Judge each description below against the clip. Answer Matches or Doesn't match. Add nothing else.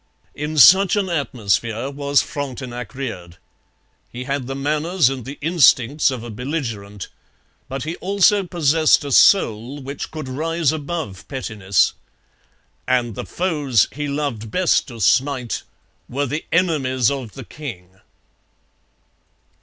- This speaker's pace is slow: Matches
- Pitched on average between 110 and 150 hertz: Matches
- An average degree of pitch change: Matches